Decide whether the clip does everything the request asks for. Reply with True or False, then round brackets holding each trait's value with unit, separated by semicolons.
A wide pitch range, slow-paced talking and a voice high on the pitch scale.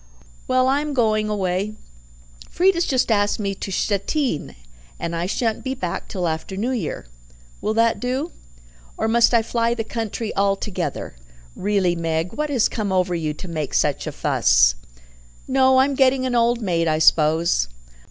False (5.8 semitones; 170 wpm; 215 Hz)